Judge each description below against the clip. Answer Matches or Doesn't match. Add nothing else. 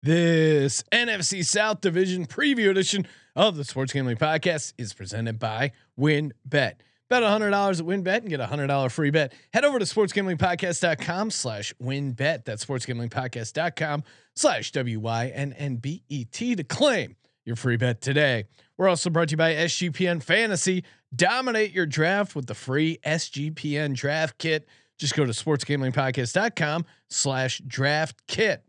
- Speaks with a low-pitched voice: Doesn't match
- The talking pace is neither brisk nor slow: Matches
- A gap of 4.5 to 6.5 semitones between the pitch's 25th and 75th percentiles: Matches